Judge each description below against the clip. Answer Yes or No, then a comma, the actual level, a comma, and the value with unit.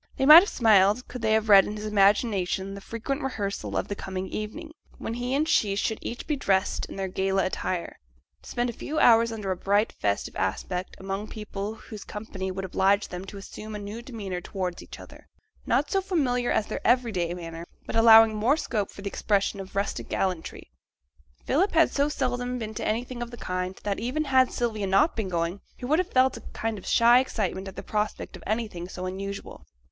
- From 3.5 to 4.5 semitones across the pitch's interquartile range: Yes, average, 4.0 semitones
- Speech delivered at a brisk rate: Yes, fast, 215 wpm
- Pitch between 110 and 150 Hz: No, high, 210 Hz